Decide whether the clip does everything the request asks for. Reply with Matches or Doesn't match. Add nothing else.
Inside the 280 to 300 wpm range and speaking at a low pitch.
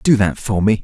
Matches